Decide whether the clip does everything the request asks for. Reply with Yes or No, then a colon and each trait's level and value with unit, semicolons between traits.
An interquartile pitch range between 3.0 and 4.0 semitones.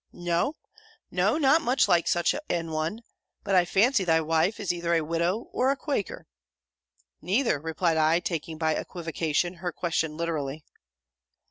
Yes: average, 3.5 semitones